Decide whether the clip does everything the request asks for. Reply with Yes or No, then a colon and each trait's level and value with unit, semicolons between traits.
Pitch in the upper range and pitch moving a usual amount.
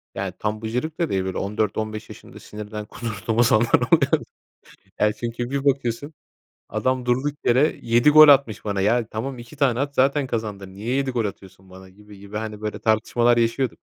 No: low, 115 Hz; average, 3.5 semitones